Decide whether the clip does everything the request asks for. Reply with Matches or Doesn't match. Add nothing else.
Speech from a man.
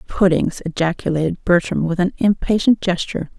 Doesn't match